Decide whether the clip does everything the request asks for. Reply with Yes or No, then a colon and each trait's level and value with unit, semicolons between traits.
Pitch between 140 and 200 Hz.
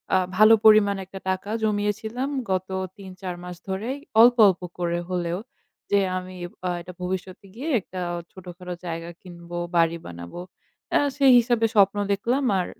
Yes: high, 190 Hz